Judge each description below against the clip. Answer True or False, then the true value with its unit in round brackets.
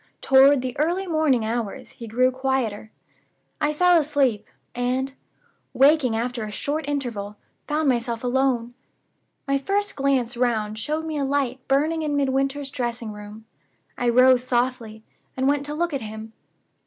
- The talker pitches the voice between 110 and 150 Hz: False (260 Hz)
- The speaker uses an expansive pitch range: False (3.5 semitones)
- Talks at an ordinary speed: True (150 wpm)